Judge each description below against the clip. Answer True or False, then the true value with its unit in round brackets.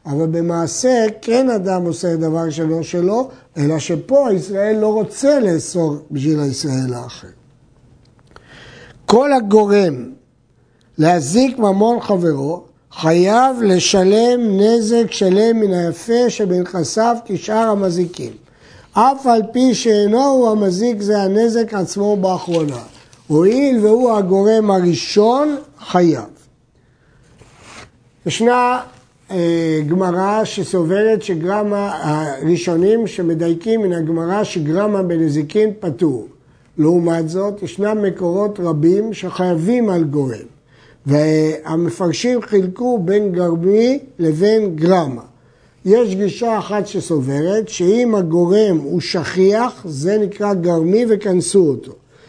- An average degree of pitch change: True (5.0 semitones)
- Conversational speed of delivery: False (95 wpm)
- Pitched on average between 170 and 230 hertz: True (185 Hz)